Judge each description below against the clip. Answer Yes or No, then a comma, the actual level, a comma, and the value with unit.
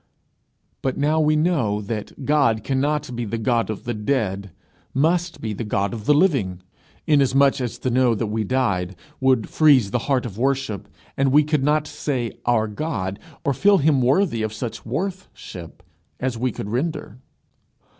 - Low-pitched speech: Yes, low, 130 Hz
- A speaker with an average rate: Yes, average, 175 wpm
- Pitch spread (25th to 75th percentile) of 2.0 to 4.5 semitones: No, average, 5.1 semitones